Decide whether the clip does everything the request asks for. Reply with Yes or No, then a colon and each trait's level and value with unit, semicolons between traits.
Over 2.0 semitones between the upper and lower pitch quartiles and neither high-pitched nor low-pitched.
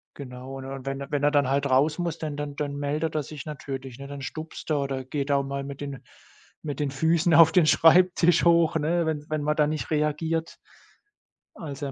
Yes: narrow, 2.4 semitones; medium, 145 Hz